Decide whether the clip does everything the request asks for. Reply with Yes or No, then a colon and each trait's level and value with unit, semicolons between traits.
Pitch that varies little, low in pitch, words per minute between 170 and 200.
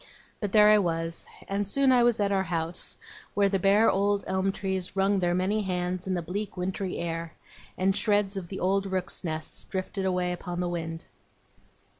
No: narrow, 2.1 semitones; high, 190 Hz; average, 190 wpm